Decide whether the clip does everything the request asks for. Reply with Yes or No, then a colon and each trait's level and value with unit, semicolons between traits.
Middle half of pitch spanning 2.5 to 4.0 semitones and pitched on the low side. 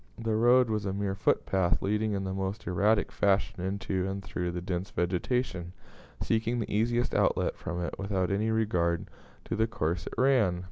Yes: average, 3.4 semitones; low, 100 Hz